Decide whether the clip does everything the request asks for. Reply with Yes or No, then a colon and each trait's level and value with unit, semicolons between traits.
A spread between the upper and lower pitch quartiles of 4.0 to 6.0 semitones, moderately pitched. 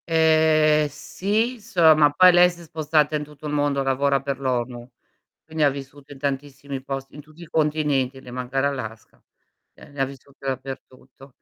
No: narrow, 2.5 semitones; medium, 145 Hz